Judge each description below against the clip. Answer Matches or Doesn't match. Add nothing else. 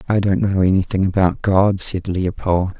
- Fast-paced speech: Doesn't match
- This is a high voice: Doesn't match